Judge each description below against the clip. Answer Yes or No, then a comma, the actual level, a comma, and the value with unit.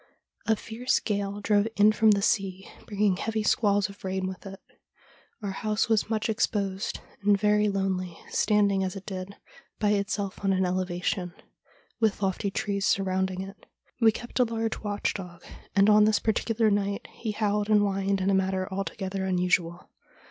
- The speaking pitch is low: No, high, 200 Hz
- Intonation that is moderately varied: No, narrow, 1.8 semitones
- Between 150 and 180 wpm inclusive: Yes, average, 170 wpm